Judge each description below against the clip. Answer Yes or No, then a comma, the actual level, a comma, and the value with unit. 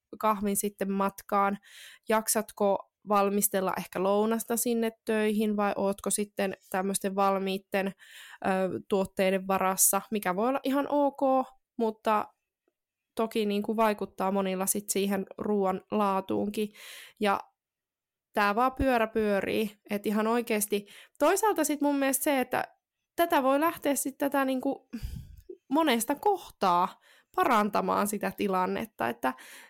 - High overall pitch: Yes, high, 215 Hz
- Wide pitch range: No, average, 4.6 semitones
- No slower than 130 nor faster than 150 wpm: No, average, 120 wpm